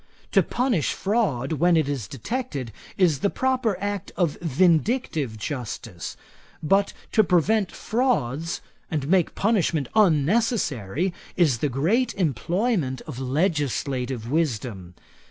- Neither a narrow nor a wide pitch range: No, wide, 7.3 semitones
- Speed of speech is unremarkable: No, slow, 115 wpm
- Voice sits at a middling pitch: Yes, medium, 160 Hz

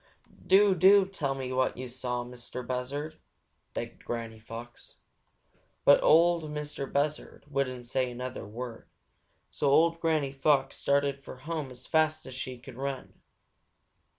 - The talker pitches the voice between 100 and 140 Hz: Yes, low, 135 Hz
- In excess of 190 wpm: No, average, 145 wpm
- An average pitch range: Yes, average, 3.3 semitones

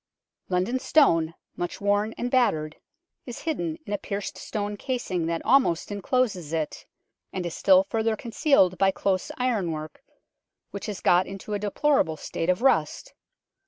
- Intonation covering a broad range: Yes, wide, 5.8 semitones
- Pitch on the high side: Yes, high, 205 Hz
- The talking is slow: No, average, 150 wpm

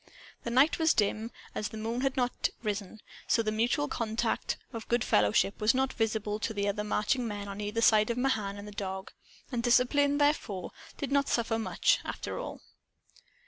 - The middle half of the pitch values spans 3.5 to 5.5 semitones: No, average, 3.1 semitones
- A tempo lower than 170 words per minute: No, average, 185 wpm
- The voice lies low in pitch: No, high, 225 Hz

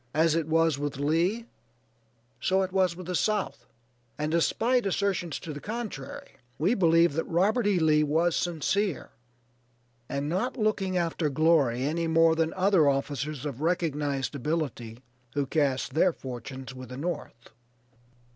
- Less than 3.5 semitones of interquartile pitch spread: No, average, 4.3 semitones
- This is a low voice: No, medium, 165 Hz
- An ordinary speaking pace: Yes, average, 145 wpm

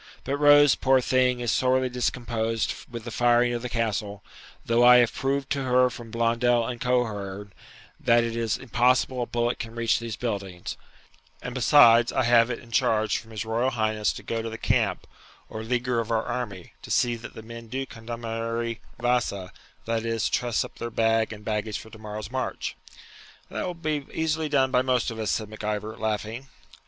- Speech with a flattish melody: Yes, narrow, 2.0 semitones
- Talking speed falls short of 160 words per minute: No, average, 190 wpm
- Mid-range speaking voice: No, low, 115 Hz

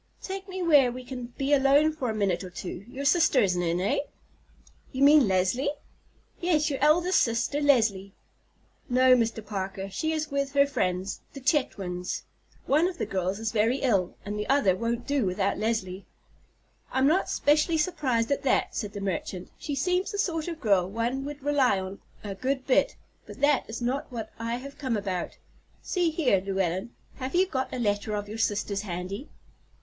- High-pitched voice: Yes, high, 245 Hz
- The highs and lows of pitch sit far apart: Yes, wide, 6.4 semitones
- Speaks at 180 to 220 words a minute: Yes, average, 185 wpm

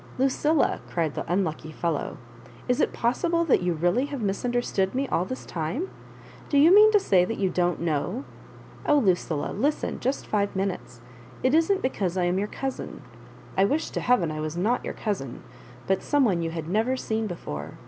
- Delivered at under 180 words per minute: No, average, 190 wpm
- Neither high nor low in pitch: No, high, 200 Hz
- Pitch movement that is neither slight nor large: No, wide, 7.2 semitones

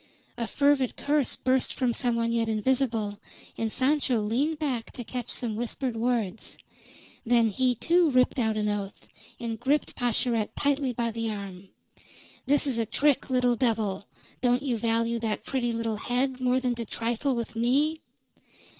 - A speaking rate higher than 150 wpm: Yes, average, 165 wpm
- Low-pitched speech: No, high, 240 Hz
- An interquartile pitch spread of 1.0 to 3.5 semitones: Yes, narrow, 2.6 semitones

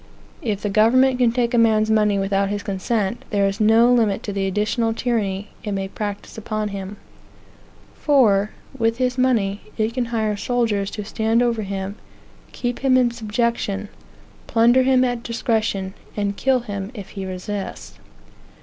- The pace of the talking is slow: No, average, 160 wpm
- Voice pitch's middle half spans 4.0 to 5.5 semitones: No, average, 3.0 semitones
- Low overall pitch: No, high, 215 Hz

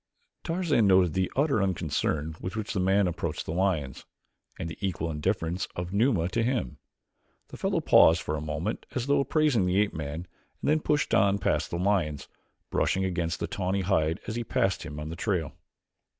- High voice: No, very low, 95 Hz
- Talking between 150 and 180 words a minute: No, average, 190 wpm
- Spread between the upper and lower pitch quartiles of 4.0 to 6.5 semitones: Yes, average, 4.3 semitones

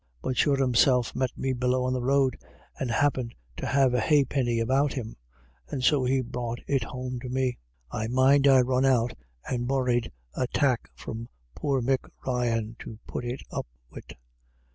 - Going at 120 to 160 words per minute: No, average, 175 wpm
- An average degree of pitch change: No, narrow, 1.7 semitones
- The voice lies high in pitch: No, low, 125 Hz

